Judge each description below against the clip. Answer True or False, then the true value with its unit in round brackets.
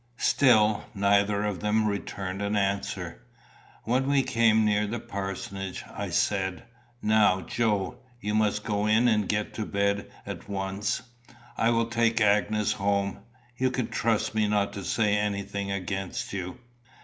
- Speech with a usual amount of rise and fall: False (1.6 semitones)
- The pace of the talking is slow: False (150 wpm)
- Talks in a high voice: False (105 Hz)